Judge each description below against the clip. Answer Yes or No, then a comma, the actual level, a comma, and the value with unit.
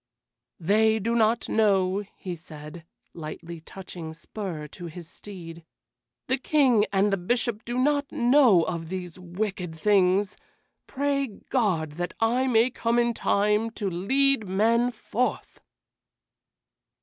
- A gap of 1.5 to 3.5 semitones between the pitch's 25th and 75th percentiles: No, average, 5.2 semitones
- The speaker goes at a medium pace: No, slow, 125 wpm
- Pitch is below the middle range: No, high, 205 Hz